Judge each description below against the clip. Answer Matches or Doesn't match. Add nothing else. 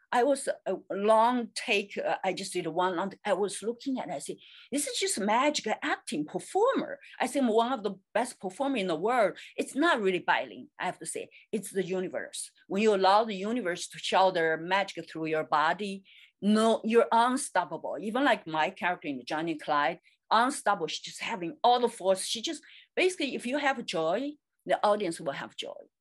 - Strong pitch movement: Matches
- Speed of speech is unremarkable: Matches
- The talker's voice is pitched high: Matches